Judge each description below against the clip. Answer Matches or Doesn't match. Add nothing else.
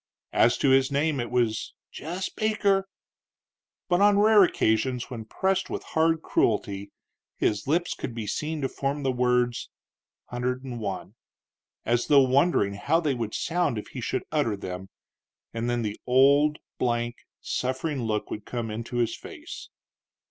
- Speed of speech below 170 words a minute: Matches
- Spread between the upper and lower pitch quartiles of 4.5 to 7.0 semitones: Matches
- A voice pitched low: Matches